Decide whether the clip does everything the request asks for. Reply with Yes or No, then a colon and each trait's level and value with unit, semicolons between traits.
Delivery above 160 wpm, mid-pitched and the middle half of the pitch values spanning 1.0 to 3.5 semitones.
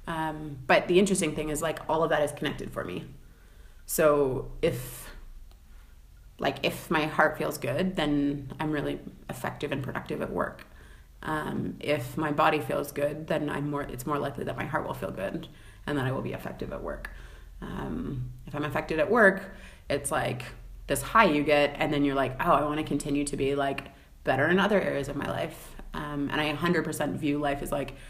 Yes: fast, 205 wpm; medium, 145 Hz; average, 2.9 semitones